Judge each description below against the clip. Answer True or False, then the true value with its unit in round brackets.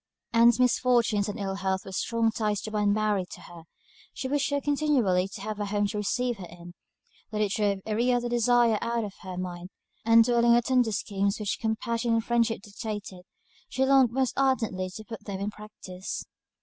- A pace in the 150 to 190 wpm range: False (200 wpm)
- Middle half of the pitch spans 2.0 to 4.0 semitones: True (3.1 semitones)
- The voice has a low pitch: False (215 Hz)